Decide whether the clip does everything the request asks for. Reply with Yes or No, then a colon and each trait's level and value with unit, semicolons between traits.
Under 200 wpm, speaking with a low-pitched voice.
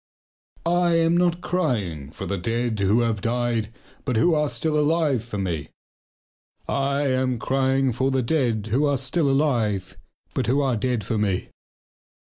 Yes: average, 160 wpm; low, 125 Hz